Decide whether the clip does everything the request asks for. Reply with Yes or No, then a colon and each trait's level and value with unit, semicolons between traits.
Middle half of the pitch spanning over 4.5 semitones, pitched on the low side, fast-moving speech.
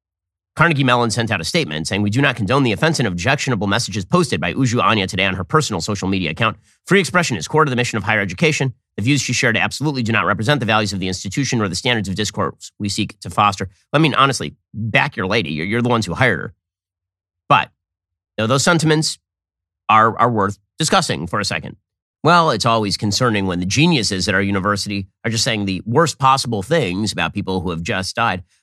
Yes: wide, 5.6 semitones; low, 110 Hz; fast, 225 wpm